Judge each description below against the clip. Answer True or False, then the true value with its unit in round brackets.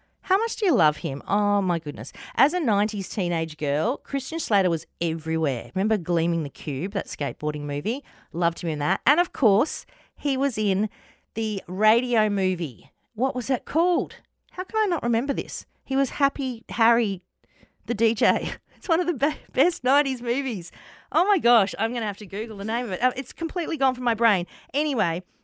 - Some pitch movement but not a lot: False (7.5 semitones)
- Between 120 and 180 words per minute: False (190 wpm)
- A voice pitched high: True (220 Hz)